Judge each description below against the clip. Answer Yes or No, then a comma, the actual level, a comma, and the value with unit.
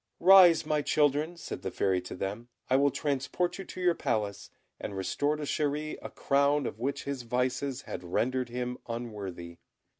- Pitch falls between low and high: No, low, 130 Hz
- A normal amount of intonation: Yes, average, 4.8 semitones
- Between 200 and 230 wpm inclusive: No, average, 175 wpm